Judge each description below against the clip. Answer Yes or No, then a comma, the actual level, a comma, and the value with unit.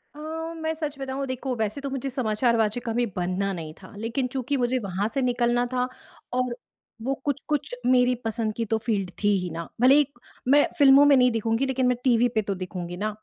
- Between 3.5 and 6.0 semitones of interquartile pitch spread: Yes, average, 3.8 semitones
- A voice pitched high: Yes, high, 245 Hz